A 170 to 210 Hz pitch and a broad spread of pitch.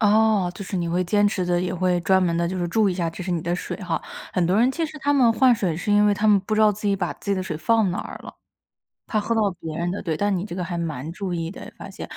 No: medium, 185 Hz; average, 3.3 semitones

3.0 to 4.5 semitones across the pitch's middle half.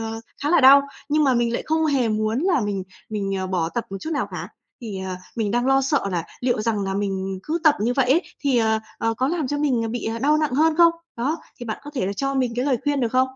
No: average, 5.0 semitones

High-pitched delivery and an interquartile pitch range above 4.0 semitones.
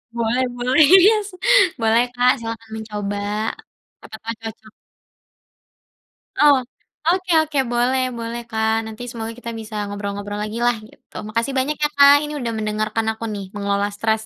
No: high, 225 Hz; average, 2.7 semitones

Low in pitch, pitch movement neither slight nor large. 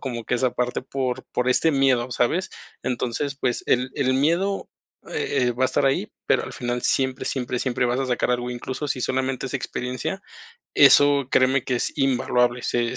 No: low, 130 Hz; narrow, 1.8 semitones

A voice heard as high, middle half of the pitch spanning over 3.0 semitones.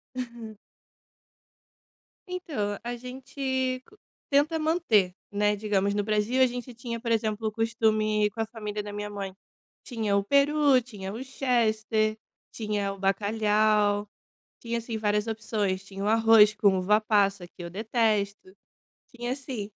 No: high, 215 Hz; average, 2.7 semitones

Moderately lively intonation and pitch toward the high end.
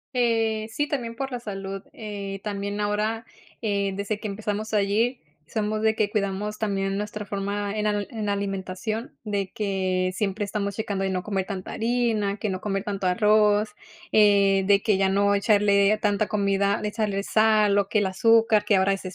No: narrow, 1.5 semitones; high, 205 Hz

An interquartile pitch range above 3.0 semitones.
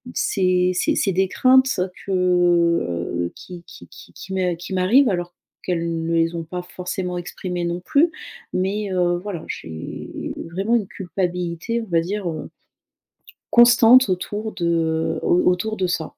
No: narrow, 2.4 semitones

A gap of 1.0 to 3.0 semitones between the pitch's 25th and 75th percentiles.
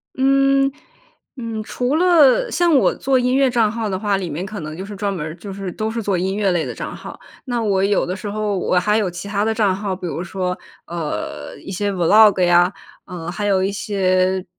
No: average, 3.7 semitones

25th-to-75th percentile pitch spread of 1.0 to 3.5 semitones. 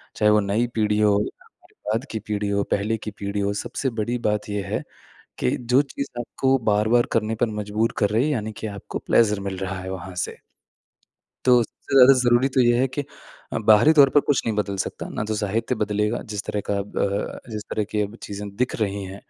Yes: average, 2.9 semitones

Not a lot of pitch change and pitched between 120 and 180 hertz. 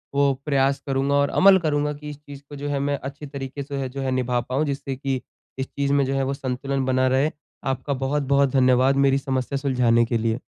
Yes: narrow, 1.5 semitones; low, 135 Hz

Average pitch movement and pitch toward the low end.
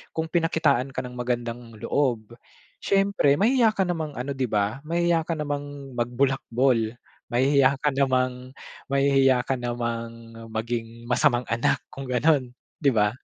Yes: average, 3.2 semitones; low, 130 Hz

